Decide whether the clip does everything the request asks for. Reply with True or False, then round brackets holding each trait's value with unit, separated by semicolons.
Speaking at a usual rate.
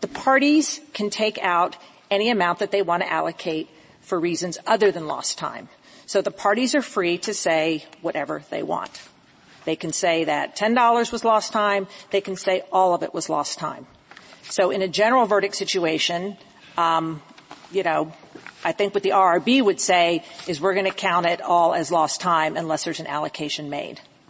True (190 wpm)